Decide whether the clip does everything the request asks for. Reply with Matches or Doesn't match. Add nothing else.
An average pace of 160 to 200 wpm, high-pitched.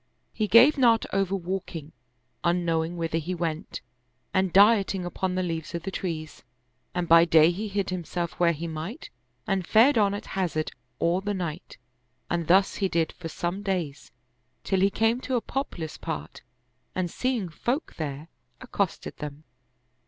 Doesn't match